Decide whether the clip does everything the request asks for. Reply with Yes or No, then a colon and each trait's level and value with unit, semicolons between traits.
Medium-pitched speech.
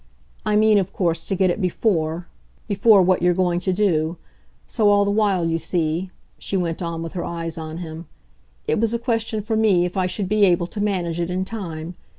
Yes: medium, 180 Hz